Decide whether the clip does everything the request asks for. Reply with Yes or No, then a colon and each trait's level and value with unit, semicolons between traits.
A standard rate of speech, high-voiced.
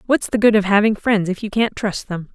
No: fast, 280 wpm; high, 205 Hz